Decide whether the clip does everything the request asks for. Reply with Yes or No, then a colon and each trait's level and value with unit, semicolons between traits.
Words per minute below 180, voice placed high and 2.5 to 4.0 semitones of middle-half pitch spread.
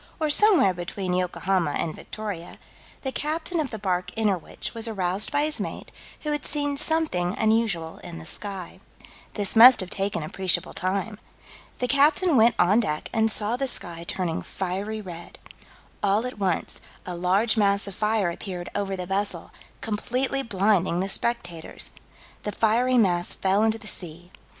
No: average, 160 wpm; high, 205 Hz; average, 4.5 semitones